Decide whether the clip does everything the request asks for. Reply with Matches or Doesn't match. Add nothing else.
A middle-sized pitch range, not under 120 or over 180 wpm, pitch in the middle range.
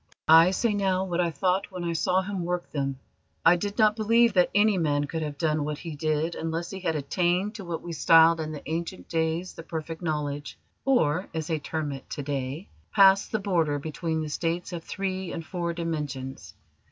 Doesn't match